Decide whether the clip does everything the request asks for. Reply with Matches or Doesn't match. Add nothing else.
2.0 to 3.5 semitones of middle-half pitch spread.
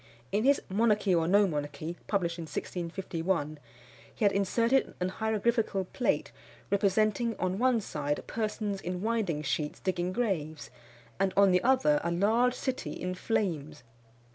Doesn't match